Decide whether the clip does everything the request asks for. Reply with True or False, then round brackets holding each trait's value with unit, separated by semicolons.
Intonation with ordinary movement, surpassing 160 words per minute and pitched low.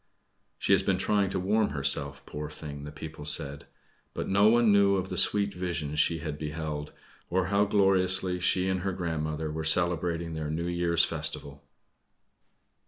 True (3.9 semitones; 170 wpm; 85 Hz)